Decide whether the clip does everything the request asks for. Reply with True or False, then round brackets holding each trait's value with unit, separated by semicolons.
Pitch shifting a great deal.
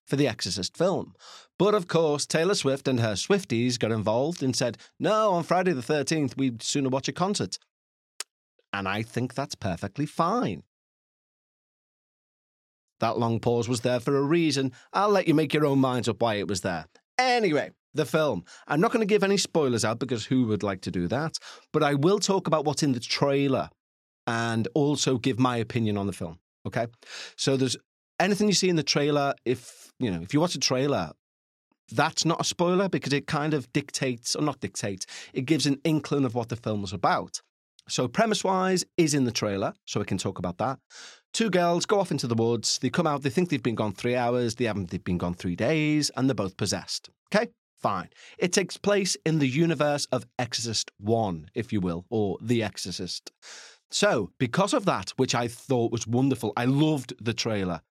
True (5.8 semitones)